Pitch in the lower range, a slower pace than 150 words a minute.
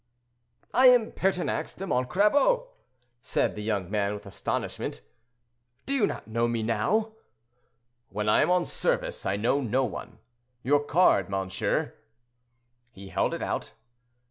Yes: low, 125 Hz; average, 140 wpm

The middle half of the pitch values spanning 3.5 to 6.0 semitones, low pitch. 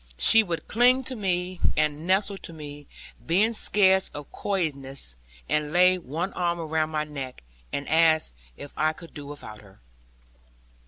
No: average, 4.2 semitones; medium, 160 Hz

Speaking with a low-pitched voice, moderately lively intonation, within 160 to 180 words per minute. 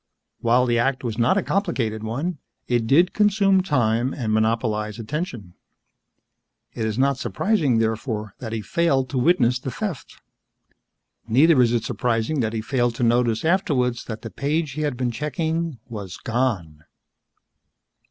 No: low, 125 Hz; average, 5.0 semitones; average, 150 wpm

